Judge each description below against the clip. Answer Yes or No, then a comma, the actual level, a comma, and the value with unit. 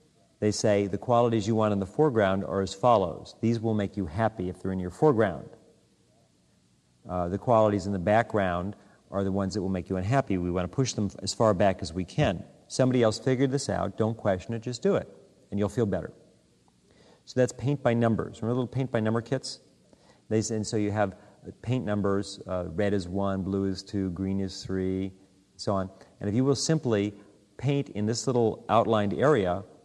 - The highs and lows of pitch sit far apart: No, average, 3.2 semitones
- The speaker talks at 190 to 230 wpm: Yes, fast, 205 wpm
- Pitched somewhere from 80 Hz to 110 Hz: Yes, low, 105 Hz